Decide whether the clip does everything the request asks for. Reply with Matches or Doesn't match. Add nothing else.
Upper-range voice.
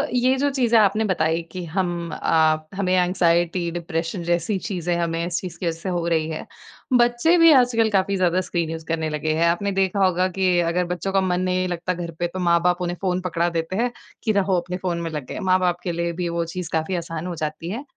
Doesn't match